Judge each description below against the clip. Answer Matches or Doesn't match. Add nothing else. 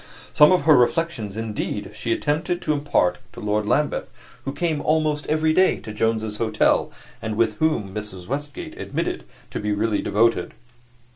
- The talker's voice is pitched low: Matches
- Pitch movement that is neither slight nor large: Doesn't match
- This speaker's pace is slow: Doesn't match